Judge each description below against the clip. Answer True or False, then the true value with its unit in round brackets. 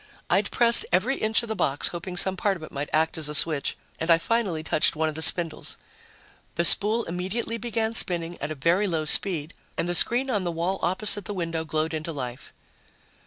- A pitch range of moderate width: True (4.7 semitones)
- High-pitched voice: False (175 Hz)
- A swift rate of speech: True (215 wpm)